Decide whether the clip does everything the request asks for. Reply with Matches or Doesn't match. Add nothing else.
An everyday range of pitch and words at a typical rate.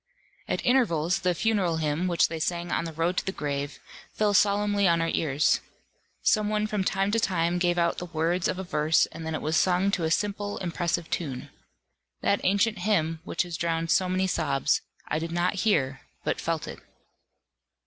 Matches